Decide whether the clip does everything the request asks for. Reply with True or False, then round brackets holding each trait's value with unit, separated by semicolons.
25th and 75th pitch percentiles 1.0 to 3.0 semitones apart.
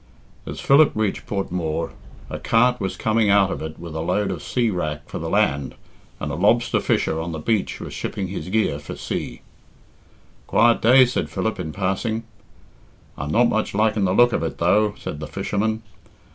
False (5.0 semitones)